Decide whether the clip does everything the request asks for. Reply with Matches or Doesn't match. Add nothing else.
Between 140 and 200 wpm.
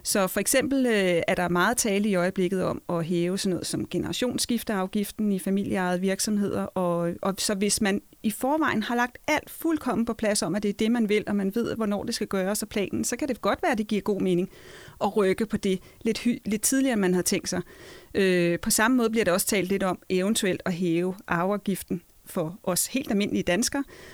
Doesn't match